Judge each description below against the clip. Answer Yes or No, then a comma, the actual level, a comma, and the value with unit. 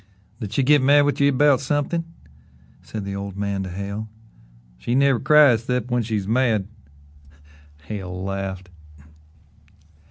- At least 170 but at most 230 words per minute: No, slow, 135 wpm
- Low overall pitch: Yes, low, 110 Hz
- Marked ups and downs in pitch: Yes, wide, 5.8 semitones